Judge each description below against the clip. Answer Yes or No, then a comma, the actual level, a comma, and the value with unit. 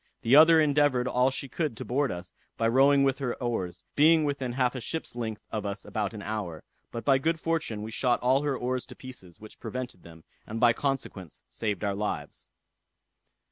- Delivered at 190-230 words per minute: Yes, average, 200 wpm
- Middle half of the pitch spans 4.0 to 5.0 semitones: Yes, average, 4.5 semitones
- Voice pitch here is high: No, low, 125 Hz